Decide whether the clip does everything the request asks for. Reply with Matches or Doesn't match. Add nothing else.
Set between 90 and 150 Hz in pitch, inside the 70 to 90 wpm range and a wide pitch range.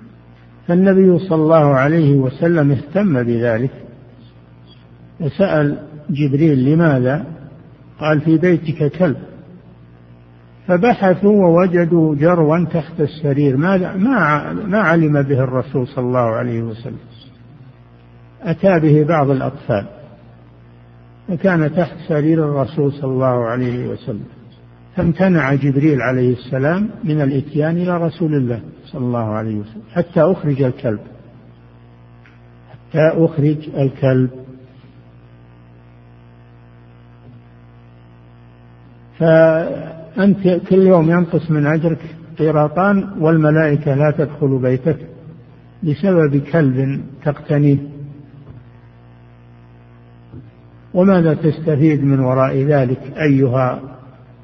Matches